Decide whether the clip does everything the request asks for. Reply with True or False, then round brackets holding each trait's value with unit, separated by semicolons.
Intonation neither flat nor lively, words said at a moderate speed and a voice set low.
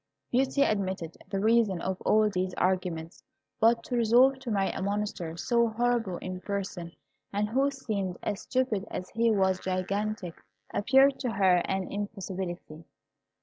False (3.9 semitones; 150 wpm; 200 Hz)